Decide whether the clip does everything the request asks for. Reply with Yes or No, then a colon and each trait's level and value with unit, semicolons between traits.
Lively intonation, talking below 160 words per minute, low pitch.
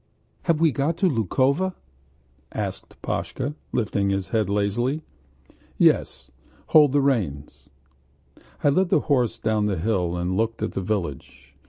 Yes: wide, 6.5 semitones; average, 140 wpm; low, 115 Hz